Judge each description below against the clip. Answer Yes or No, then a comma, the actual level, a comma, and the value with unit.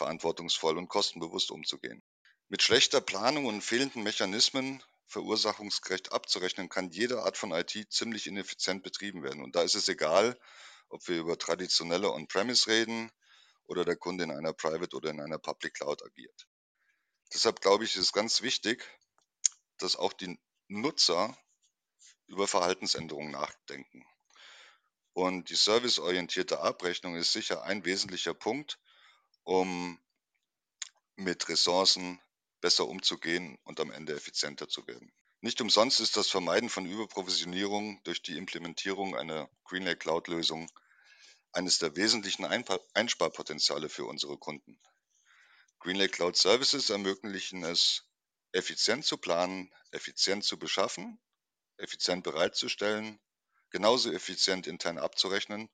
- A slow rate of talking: Yes, slow, 120 wpm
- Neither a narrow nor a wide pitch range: Yes, average, 3.4 semitones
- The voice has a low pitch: Yes, low, 100 Hz